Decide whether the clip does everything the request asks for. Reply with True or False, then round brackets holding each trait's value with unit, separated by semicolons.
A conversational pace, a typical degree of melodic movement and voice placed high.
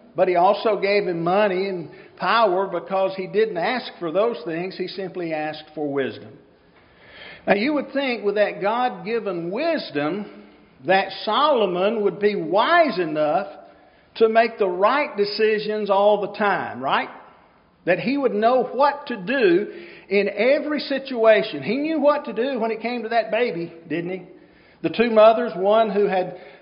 True (165 wpm; 4.6 semitones; 210 Hz)